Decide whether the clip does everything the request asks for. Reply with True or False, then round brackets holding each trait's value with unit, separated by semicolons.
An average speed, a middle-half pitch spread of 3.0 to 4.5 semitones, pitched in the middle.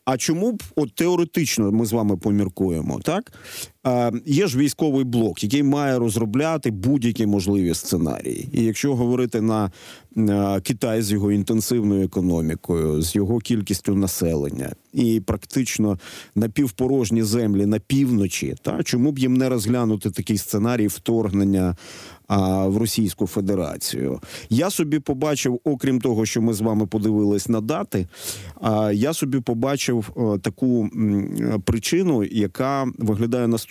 False (130 wpm; 4.1 semitones; 110 Hz)